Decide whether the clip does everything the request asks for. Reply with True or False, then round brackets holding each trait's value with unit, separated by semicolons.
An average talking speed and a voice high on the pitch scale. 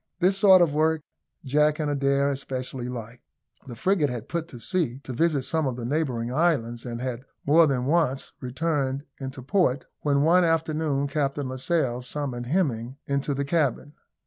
False (170 wpm; 140 Hz)